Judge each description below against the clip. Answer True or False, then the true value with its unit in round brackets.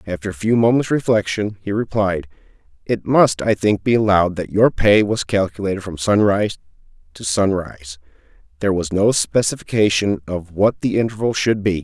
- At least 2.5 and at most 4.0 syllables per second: False (5.3 syllables/s)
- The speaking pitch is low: True (100 Hz)